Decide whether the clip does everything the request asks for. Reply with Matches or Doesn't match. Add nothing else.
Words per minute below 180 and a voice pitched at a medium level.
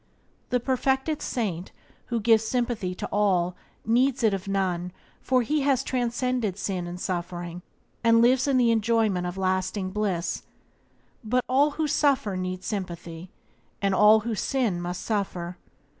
Doesn't match